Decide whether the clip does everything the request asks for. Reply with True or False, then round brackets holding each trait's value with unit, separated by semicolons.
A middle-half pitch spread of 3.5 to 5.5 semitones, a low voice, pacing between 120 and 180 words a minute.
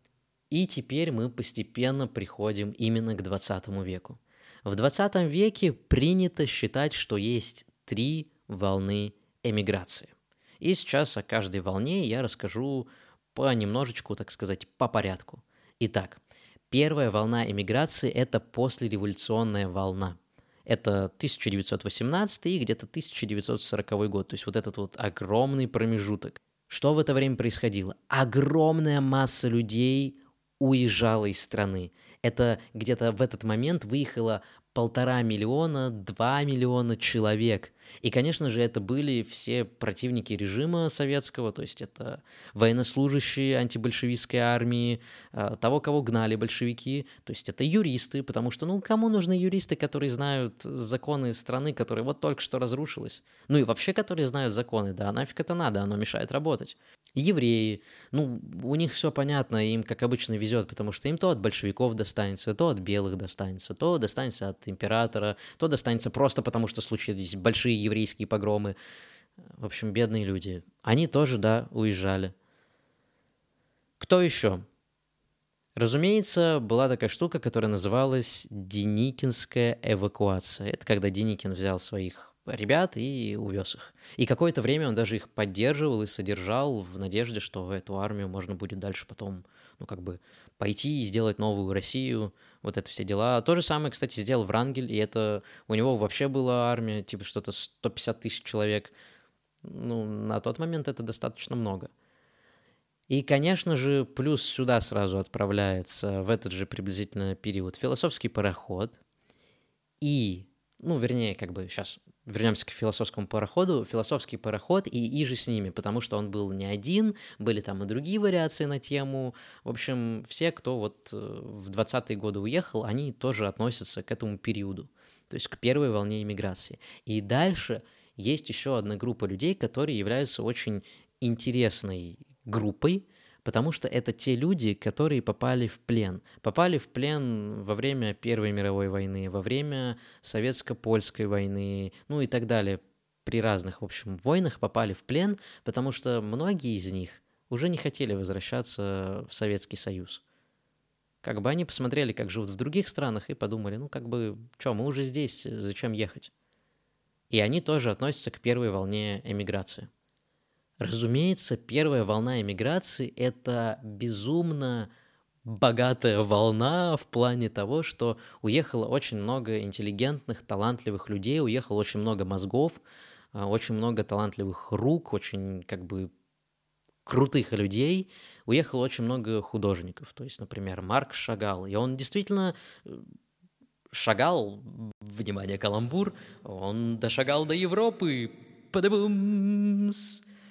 True (4.7 semitones; 115 Hz; 140 wpm)